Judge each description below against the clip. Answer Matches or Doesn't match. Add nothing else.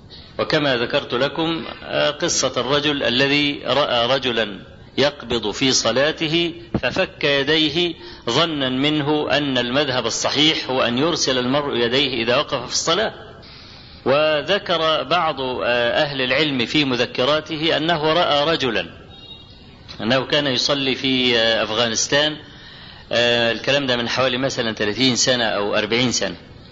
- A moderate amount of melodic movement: Matches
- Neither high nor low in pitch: Doesn't match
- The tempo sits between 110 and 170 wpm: Matches